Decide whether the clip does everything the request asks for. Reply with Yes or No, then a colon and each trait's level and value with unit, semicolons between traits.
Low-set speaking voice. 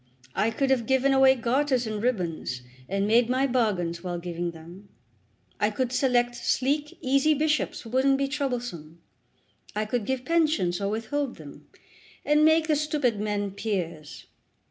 No: high, 240 Hz